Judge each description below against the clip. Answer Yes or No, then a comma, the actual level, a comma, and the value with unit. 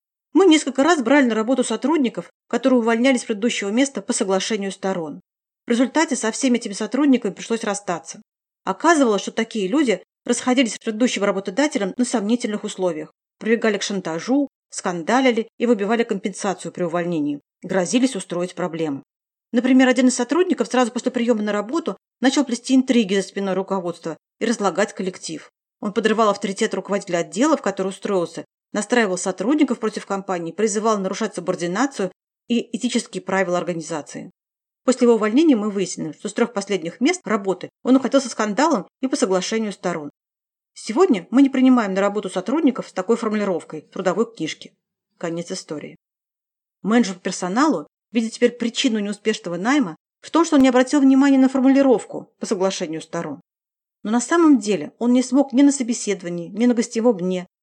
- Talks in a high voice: Yes, high, 220 Hz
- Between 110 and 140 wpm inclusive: No, average, 155 wpm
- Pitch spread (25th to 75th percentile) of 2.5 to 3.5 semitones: No, average, 4.8 semitones